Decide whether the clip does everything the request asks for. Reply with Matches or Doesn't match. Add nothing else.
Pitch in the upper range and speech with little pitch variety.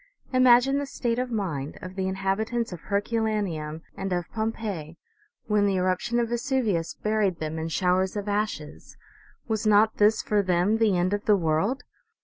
Doesn't match